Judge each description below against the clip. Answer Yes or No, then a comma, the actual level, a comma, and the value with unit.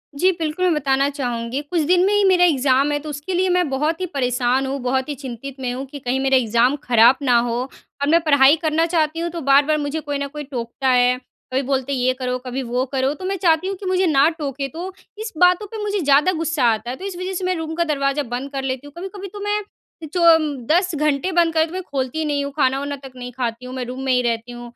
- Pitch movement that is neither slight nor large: Yes, average, 4.5 semitones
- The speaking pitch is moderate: No, very high, 285 Hz